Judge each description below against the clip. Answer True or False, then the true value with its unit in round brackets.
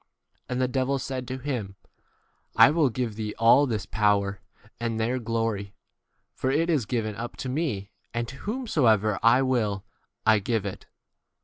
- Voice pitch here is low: True (115 Hz)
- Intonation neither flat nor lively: True (3.5 semitones)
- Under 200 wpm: True (165 wpm)